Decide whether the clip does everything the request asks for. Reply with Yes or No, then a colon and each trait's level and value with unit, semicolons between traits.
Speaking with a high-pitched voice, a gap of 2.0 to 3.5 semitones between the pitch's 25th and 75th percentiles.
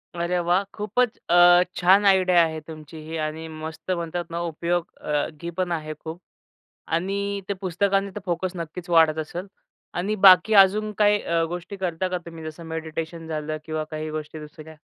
No: medium, 170 Hz; average, 2.8 semitones